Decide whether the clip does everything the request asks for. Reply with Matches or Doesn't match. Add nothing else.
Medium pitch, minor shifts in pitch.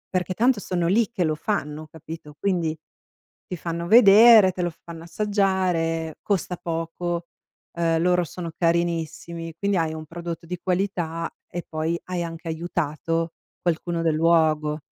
Matches